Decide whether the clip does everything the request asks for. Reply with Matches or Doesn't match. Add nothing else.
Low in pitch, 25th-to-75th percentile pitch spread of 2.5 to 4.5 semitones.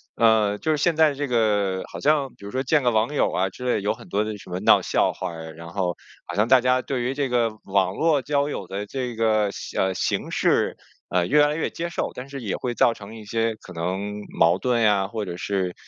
Doesn't match